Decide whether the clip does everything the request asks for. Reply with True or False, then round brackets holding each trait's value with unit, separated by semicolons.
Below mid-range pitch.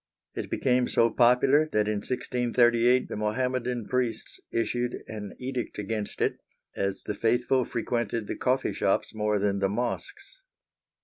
True (120 Hz)